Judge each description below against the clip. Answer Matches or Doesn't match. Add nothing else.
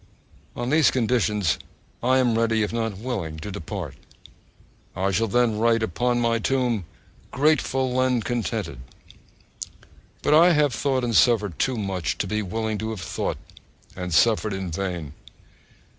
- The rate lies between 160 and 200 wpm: Doesn't match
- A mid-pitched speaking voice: Doesn't match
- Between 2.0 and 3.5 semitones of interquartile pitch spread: Doesn't match